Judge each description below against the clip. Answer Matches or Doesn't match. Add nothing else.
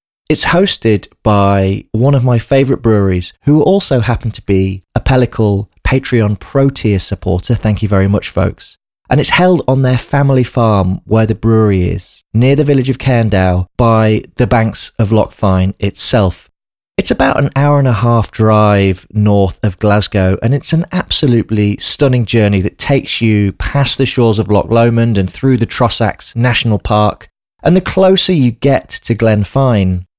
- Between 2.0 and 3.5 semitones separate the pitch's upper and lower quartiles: Doesn't match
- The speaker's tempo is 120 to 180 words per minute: Matches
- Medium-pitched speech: Doesn't match